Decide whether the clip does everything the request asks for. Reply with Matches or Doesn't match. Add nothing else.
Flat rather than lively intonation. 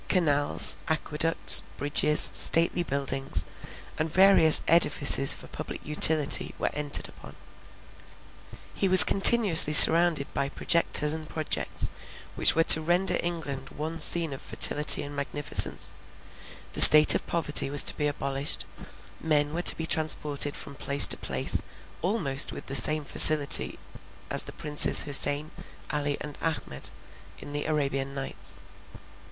Matches